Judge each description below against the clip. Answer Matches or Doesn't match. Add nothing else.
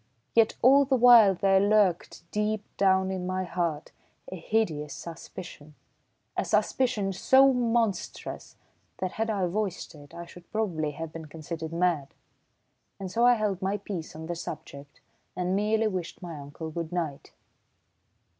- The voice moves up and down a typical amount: Matches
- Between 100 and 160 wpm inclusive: Matches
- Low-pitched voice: Doesn't match